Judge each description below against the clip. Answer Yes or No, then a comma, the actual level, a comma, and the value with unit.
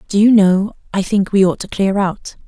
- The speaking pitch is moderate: No, high, 195 Hz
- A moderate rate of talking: No, fast, 240 wpm